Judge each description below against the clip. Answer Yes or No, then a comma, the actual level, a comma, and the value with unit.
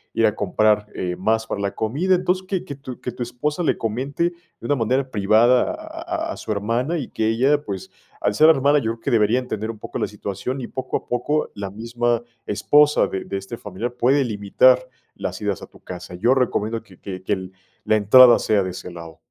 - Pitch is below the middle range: Yes, low, 120 Hz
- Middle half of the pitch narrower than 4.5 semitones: No, average, 5.2 semitones